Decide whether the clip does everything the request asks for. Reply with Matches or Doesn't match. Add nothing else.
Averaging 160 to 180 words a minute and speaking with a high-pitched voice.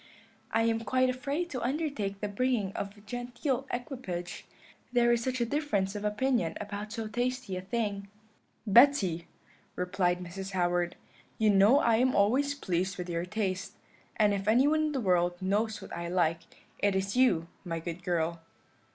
Matches